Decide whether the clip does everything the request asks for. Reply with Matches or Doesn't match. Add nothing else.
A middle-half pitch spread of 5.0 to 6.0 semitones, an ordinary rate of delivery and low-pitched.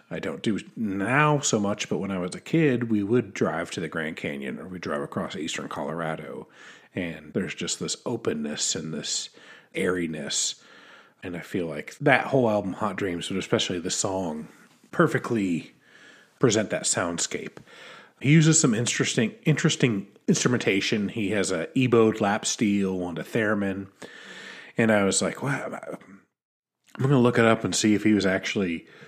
Matches